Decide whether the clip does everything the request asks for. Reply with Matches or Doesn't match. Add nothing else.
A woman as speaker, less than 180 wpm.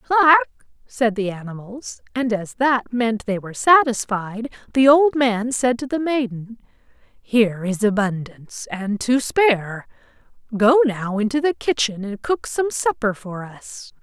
Matches